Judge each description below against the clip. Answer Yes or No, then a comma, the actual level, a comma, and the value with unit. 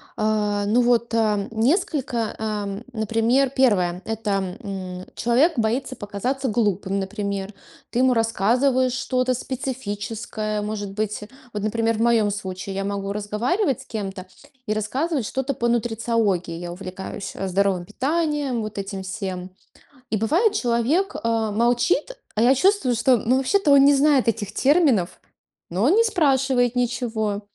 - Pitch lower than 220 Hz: No, high, 225 Hz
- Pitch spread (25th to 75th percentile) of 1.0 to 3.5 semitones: No, average, 4.2 semitones